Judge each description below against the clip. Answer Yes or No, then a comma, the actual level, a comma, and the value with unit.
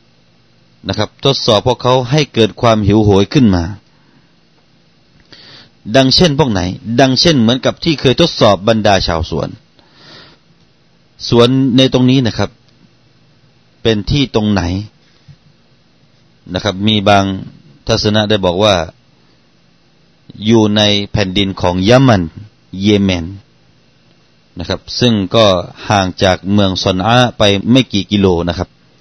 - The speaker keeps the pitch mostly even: No, average, 4.2 semitones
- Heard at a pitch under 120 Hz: Yes, low, 105 Hz